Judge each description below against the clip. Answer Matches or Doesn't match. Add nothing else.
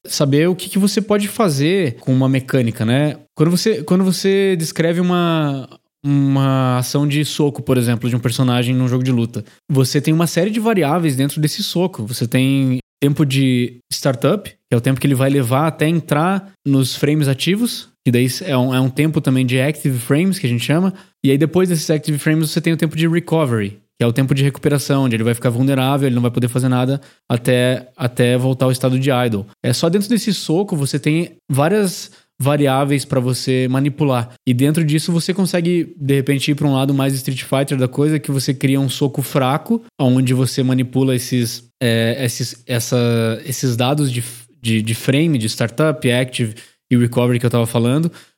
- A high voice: Doesn't match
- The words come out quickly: Matches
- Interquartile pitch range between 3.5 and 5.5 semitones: Matches